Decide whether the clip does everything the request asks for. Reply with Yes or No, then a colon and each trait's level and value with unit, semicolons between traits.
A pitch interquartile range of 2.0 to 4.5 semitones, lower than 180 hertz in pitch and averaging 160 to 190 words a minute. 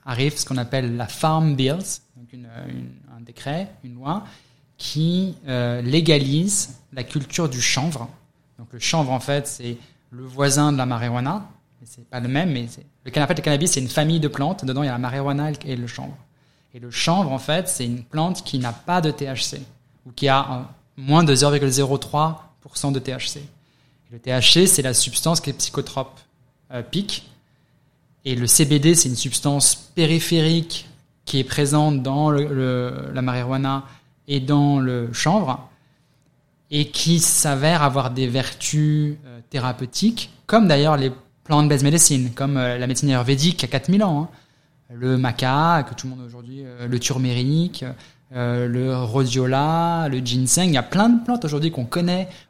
Yes: average, 3.0 semitones; medium, 140 Hz; average, 170 wpm